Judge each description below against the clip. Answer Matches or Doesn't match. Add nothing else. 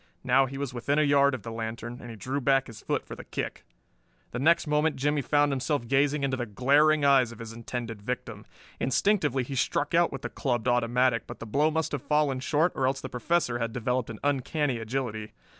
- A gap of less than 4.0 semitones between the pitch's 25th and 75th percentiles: Matches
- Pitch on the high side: Doesn't match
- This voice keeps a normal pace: Doesn't match